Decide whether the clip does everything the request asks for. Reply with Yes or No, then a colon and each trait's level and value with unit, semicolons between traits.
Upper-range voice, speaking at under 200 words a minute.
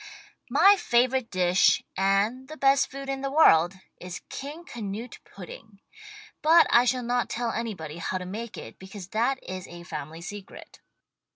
Yes: high, 225 Hz; average, 160 wpm